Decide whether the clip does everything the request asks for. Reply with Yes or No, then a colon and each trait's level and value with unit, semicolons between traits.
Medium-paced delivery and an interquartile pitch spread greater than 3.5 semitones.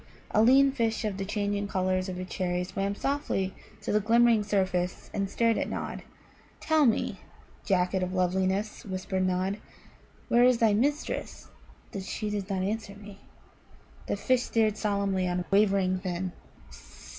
No: average, 155 wpm; average, 2.8 semitones